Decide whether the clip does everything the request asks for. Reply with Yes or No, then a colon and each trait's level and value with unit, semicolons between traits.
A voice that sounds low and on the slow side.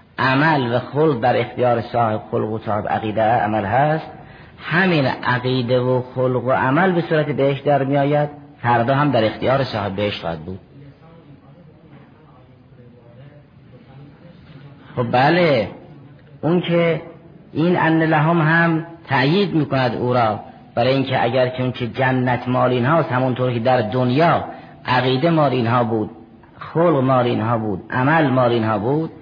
No: low, 130 Hz; average, 145 wpm